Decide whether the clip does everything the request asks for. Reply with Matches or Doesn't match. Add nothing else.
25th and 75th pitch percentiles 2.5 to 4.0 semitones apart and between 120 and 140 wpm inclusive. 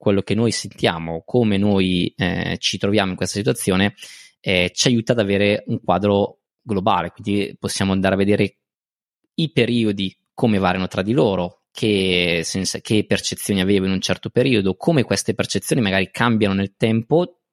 Doesn't match